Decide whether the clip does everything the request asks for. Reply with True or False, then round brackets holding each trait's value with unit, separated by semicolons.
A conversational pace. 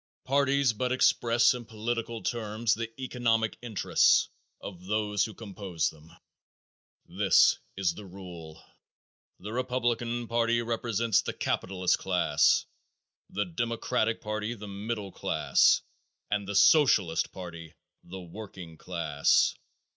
False (115 wpm)